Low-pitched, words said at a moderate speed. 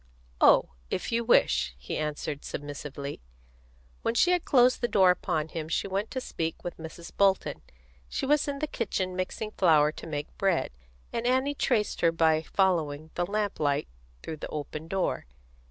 No: medium, 175 Hz; average, 170 wpm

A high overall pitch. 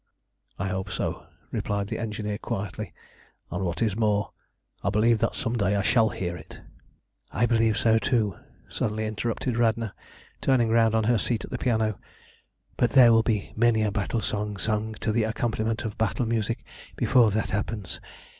No: low, 110 Hz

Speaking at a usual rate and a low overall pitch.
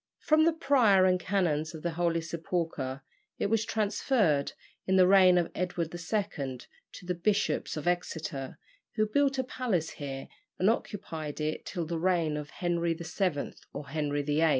No: average, 165 wpm; medium, 175 Hz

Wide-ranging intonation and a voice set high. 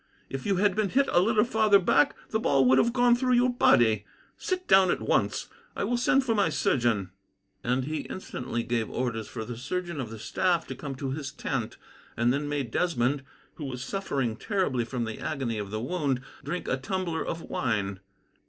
No: wide, 8.2 semitones; medium, 140 Hz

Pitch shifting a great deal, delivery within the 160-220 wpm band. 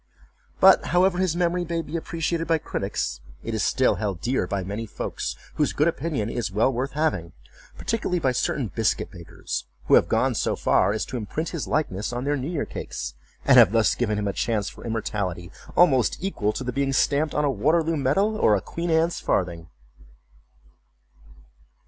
Yes: wide, 7.7 semitones; average, 185 wpm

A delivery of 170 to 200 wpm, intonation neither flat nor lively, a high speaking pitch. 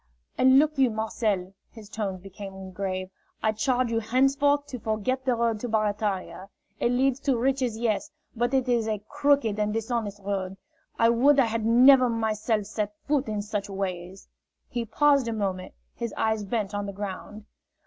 Yes: average, 175 wpm; average, 3.5 semitones; high, 220 Hz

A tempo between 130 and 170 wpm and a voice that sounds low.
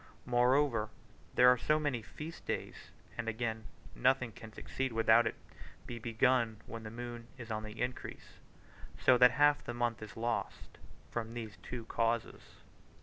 Yes: average, 155 wpm; low, 120 Hz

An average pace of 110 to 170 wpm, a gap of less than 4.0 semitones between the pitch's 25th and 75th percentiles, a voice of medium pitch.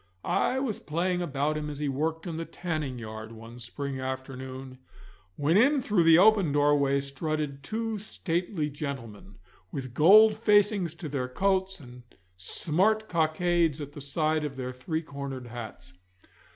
No: average, 150 wpm; average, 5.0 semitones; medium, 150 Hz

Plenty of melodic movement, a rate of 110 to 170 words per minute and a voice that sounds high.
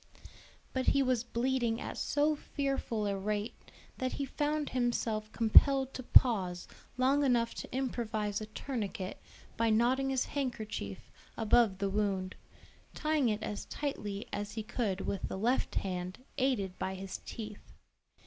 No: average, 4.3 semitones; average, 145 wpm; high, 230 Hz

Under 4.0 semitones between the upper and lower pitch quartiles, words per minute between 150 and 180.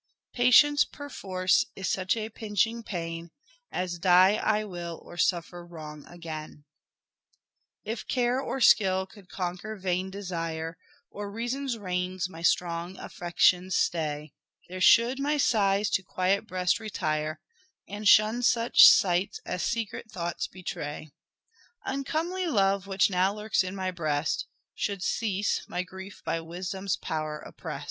No: average, 3.6 semitones; slow, 135 wpm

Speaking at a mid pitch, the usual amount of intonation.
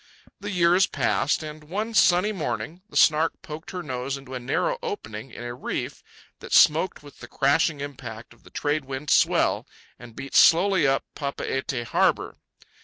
Yes: medium, 150 Hz; average, 4.9 semitones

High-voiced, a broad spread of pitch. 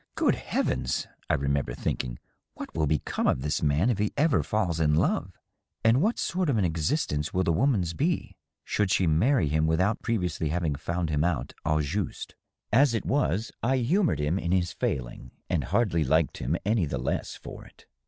No: very low, 85 Hz; wide, 6.8 semitones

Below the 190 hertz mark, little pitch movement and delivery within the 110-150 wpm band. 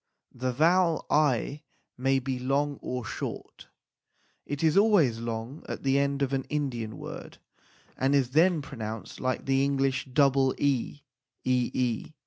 Yes: low, 135 Hz; narrow, 2.3 semitones; average, 140 wpm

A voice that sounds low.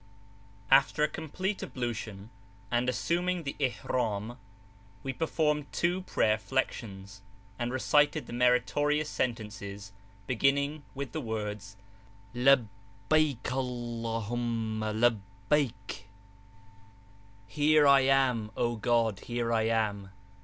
Yes: low, 120 Hz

